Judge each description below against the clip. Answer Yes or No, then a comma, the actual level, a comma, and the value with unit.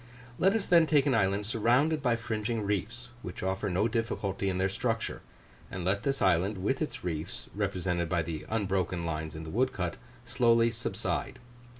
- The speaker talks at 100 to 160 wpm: No, average, 175 wpm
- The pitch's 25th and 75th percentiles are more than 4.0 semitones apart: Yes, average, 4.6 semitones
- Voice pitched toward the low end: Yes, low, 105 Hz